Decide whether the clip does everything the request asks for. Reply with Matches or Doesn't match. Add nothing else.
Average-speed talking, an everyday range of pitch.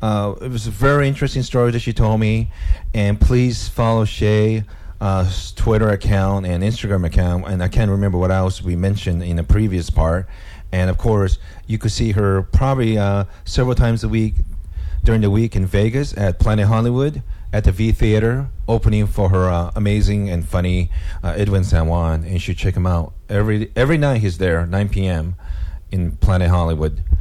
Matches